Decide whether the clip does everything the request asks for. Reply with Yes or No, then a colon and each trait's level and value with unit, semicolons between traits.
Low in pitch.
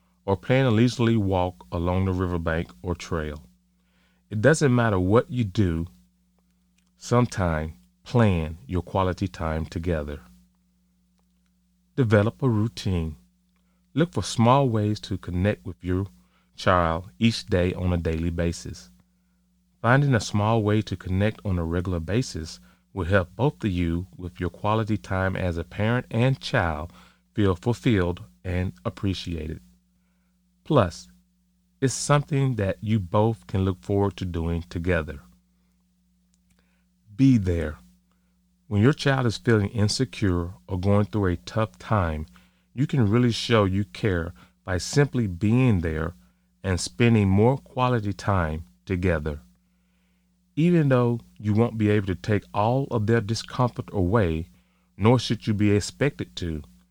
Yes: very low, 90 Hz